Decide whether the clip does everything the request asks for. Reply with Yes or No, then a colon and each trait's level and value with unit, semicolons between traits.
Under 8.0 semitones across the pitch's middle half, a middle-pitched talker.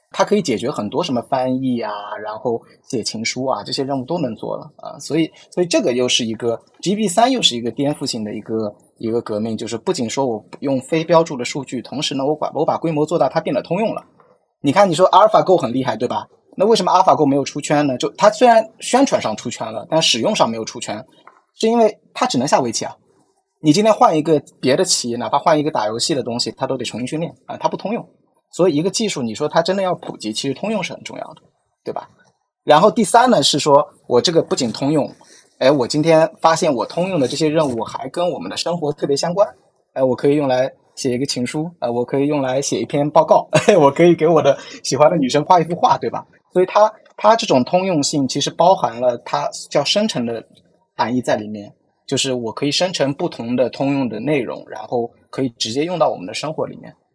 Yes: wide, 5.5 semitones; medium, 145 Hz